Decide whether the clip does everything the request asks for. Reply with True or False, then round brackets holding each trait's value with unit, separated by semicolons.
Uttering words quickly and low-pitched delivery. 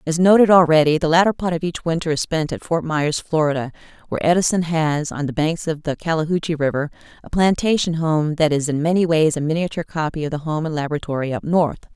False (215 wpm; 160 Hz)